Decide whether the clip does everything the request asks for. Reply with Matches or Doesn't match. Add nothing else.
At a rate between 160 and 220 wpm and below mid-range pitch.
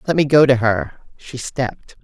Matches